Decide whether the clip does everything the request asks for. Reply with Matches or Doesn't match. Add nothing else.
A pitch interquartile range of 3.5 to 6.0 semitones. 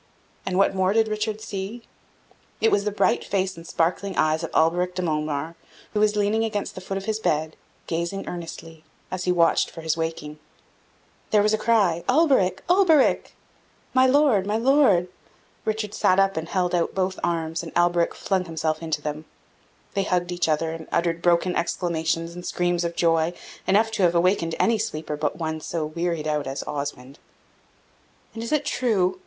Matches